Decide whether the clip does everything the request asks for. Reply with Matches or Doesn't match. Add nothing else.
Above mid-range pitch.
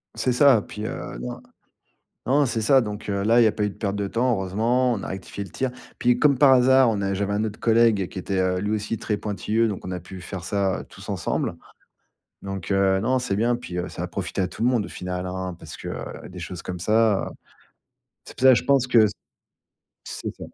Doesn't match